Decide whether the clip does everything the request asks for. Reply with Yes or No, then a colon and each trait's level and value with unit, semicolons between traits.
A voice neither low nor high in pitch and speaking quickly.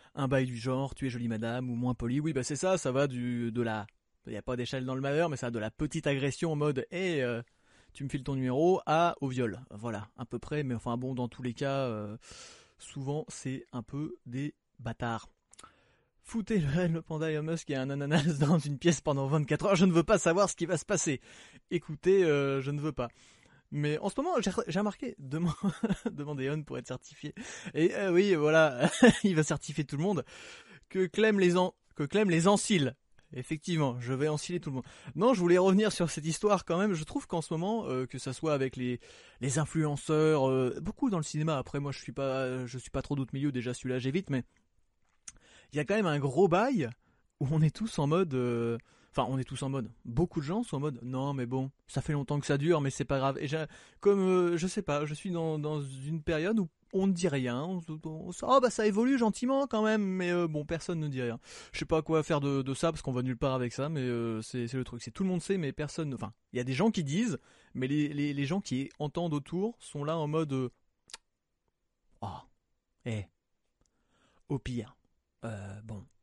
Yes: medium, 150 Hz; fast, 235 wpm